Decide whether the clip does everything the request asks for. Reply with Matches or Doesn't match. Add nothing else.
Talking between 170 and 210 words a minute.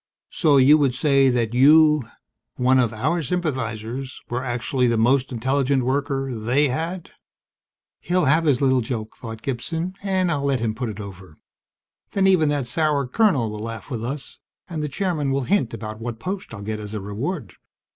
Matches